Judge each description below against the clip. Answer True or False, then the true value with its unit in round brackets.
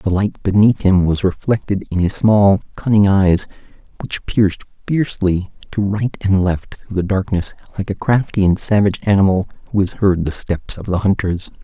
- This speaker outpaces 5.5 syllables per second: False (5.1 syllables/s)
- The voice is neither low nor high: False (100 Hz)